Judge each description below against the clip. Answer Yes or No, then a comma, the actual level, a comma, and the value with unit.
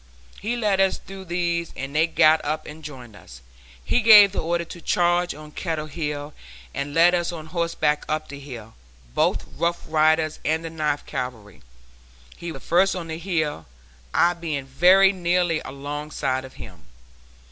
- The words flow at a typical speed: Yes, average, 170 wpm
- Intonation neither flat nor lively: Yes, average, 3.1 semitones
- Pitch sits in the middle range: Yes, medium, 160 Hz